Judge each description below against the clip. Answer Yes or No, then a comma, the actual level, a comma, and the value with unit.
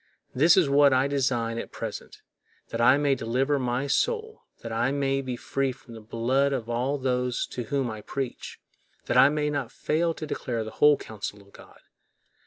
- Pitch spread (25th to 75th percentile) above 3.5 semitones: No, average, 3.2 semitones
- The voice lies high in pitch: No, low, 130 Hz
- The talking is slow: No, average, 190 wpm